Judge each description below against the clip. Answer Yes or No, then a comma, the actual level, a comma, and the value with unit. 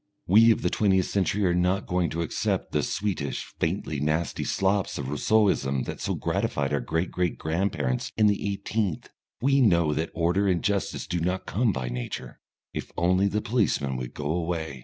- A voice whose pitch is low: Yes, very low, 90 Hz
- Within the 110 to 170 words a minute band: No, average, 180 wpm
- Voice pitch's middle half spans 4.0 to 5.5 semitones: Yes, average, 4.6 semitones